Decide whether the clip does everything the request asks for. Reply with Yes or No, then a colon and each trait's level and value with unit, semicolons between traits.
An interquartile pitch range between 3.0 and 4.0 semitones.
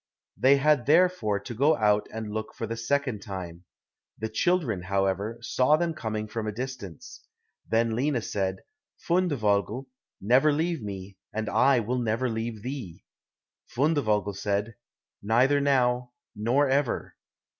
No: average, 4.8 semitones